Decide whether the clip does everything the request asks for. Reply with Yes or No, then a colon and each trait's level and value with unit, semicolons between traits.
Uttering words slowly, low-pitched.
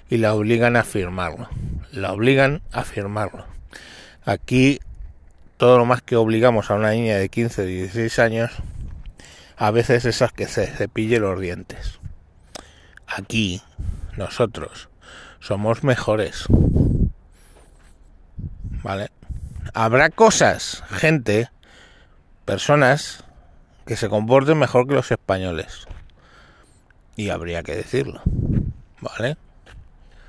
Yes: slow, 100 wpm; low, 100 Hz